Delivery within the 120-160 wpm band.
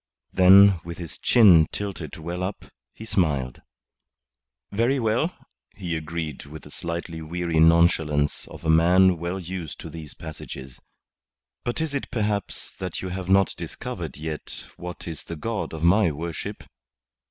Yes: average, 150 wpm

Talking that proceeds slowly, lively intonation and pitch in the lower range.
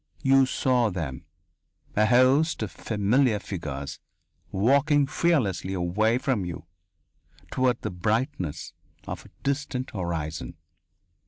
Yes: slow, 105 wpm; wide, 6.9 semitones; low, 110 Hz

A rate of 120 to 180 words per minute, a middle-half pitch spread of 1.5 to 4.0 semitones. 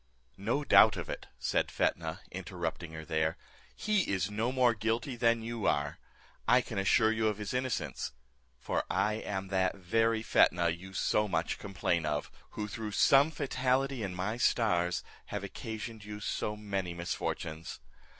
No: average, 160 wpm; average, 4.7 semitones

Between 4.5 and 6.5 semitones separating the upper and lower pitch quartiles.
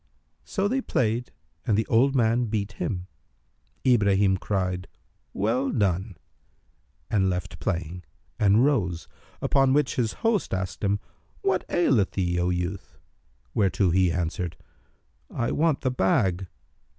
Yes: average, 5.2 semitones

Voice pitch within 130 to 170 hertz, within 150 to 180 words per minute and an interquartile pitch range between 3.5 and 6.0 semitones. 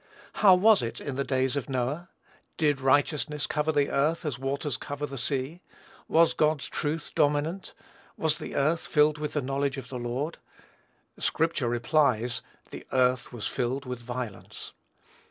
No: medium, 140 Hz; average, 160 wpm; average, 3.1 semitones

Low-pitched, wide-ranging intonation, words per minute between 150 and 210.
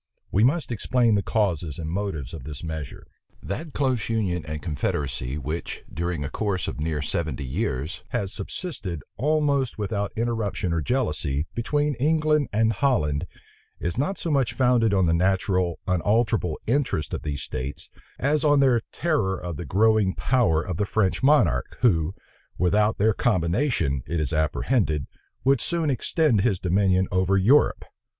Yes: low, 100 Hz; wide, 7.1 semitones; average, 155 wpm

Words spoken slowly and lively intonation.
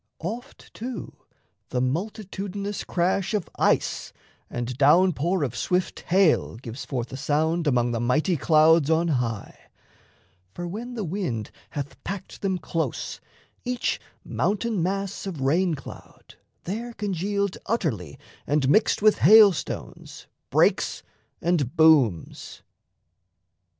Yes: slow, 120 wpm; wide, 6.4 semitones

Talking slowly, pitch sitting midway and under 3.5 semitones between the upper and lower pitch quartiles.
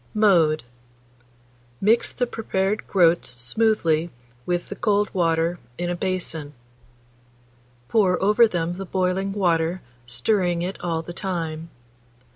Yes: slow, 115 wpm; medium, 180 Hz; average, 3.1 semitones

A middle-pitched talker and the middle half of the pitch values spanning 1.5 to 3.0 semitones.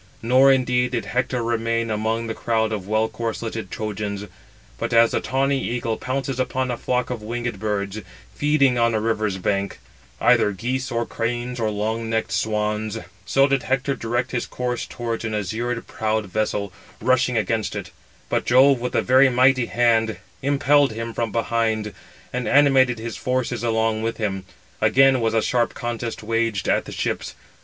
No: low, 115 Hz; narrow, 2.4 semitones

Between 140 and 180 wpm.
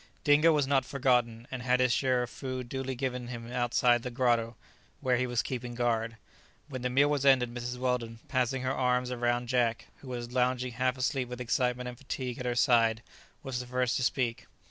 No: fast, 205 wpm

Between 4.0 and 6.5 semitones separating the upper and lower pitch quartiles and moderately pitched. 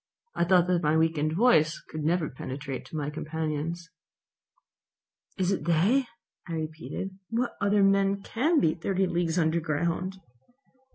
No: average, 3.6 semitones; medium, 170 Hz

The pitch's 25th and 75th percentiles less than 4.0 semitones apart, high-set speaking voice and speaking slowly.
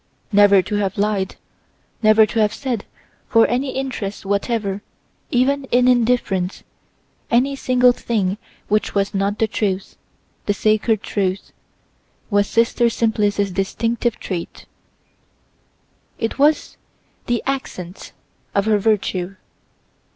Yes: average, 3.3 semitones; high, 215 Hz; slow, 115 wpm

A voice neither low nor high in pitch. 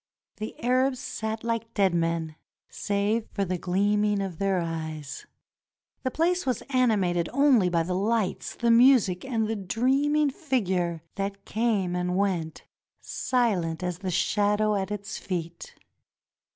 No: high, 200 Hz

